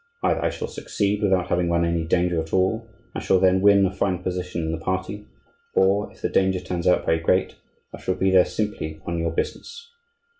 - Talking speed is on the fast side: Yes, fast, 215 wpm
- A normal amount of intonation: No, narrow, 2.2 semitones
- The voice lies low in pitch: Yes, very low, 95 Hz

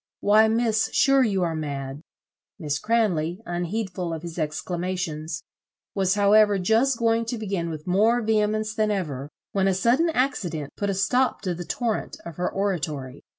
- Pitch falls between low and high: No, high, 195 Hz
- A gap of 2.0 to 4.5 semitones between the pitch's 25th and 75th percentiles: No, average, 4.9 semitones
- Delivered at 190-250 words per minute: No, average, 160 wpm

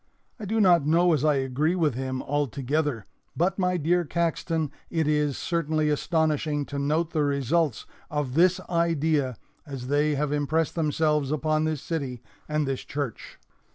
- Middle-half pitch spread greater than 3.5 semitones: No, narrow, 2.6 semitones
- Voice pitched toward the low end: No, medium, 150 Hz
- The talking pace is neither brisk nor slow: Yes, average, 155 wpm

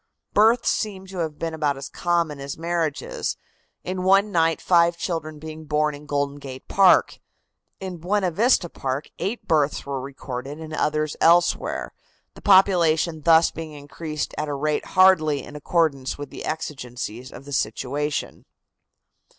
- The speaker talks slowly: No, average, 150 wpm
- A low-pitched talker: No, medium, 155 Hz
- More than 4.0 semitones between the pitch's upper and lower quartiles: No, average, 3.3 semitones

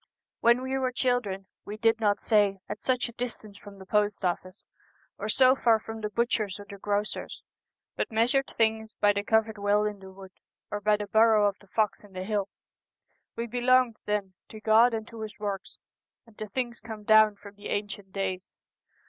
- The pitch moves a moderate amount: No, narrow, 2.0 semitones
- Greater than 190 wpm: Yes, average, 200 wpm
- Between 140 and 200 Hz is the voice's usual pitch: No, high, 215 Hz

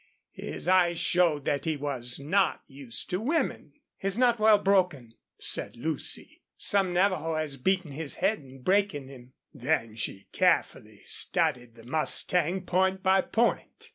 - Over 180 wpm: No, average, 145 wpm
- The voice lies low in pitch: No, medium, 160 Hz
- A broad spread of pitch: Yes, wide, 5.8 semitones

